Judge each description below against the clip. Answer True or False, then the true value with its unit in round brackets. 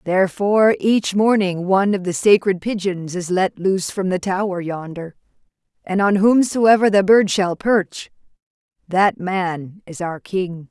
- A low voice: False (190 Hz)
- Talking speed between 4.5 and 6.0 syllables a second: False (4.3 syllables/s)